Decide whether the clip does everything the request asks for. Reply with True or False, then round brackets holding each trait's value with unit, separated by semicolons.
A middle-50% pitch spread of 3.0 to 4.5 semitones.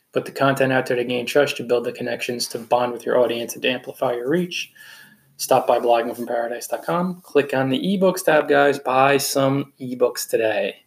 False (2.6 semitones)